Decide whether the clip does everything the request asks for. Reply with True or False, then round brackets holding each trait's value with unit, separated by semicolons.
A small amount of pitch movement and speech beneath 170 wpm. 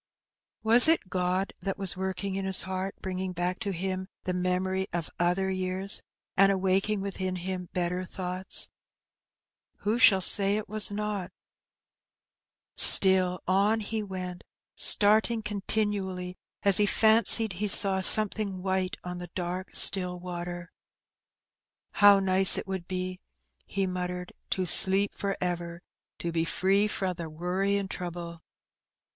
True (1.7 semitones; 140 wpm)